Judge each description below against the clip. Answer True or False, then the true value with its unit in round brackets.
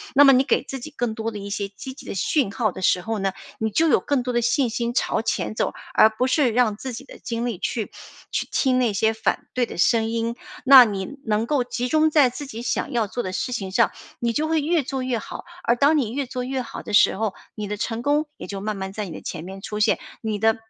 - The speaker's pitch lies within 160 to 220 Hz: False (235 Hz)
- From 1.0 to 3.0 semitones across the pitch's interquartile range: False (3.6 semitones)